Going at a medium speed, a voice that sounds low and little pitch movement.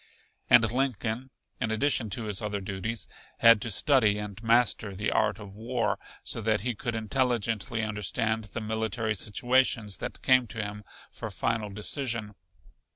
Yes: average, 155 wpm; low, 110 Hz; narrow, 2.3 semitones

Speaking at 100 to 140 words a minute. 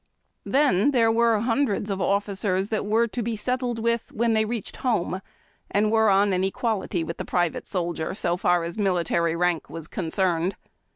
No: average, 175 wpm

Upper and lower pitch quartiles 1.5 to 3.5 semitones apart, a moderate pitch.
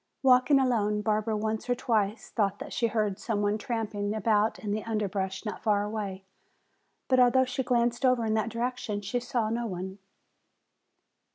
No: narrow, 2.6 semitones; high, 220 Hz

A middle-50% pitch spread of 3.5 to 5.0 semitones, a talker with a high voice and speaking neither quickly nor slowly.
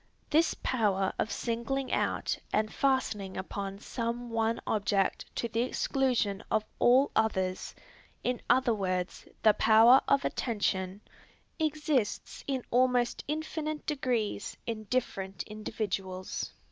No: average, 4.3 semitones; high, 225 Hz; slow, 115 wpm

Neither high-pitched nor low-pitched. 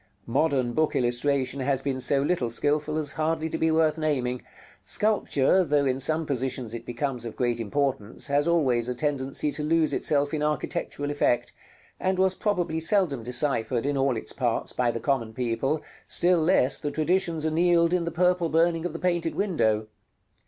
Yes: medium, 145 Hz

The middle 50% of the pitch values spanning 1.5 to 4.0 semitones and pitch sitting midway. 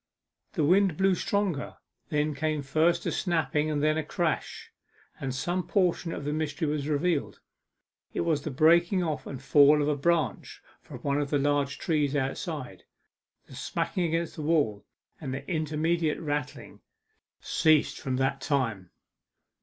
Yes: average, 2.8 semitones; medium, 150 Hz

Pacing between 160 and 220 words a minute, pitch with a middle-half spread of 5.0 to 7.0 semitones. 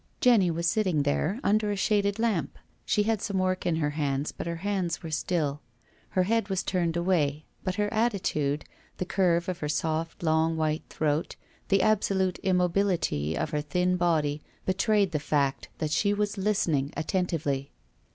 No: average, 170 wpm; average, 4.4 semitones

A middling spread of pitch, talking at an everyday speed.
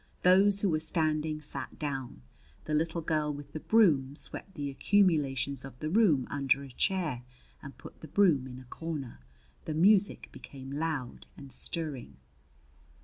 Yes: average, 3.5 semitones; average, 155 wpm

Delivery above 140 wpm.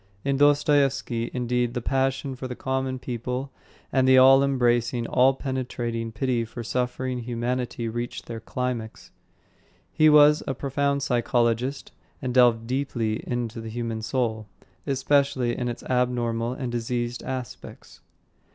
No: slow, 135 wpm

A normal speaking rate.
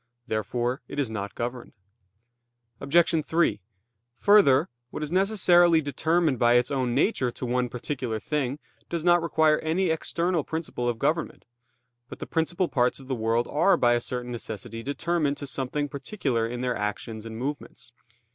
Yes: average, 160 wpm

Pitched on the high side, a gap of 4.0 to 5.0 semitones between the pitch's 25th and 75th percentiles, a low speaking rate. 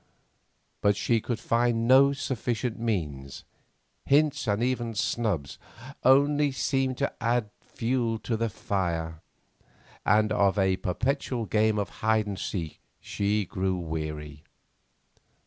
No: low, 110 Hz; average, 4.4 semitones; slow, 120 wpm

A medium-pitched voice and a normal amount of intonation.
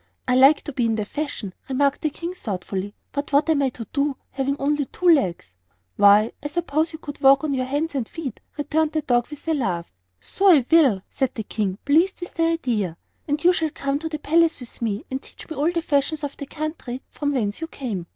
No: very high, 280 Hz; average, 4.4 semitones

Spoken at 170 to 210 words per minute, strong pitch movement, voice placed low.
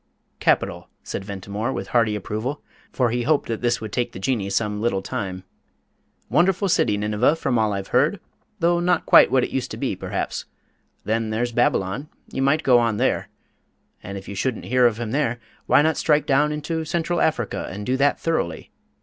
Yes: average, 190 wpm; wide, 5.9 semitones; low, 120 Hz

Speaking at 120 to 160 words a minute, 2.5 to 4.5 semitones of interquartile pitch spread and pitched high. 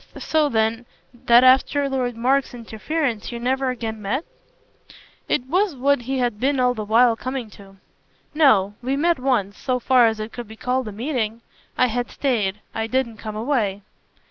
No: average, 175 wpm; average, 3.3 semitones; high, 245 Hz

